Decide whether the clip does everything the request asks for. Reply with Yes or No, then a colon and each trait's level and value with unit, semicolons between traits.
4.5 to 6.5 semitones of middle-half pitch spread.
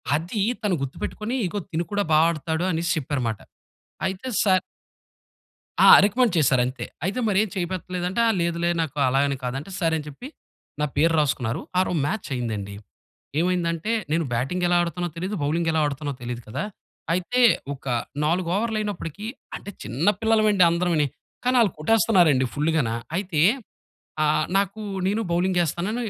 Yes: average, 4.8 semitones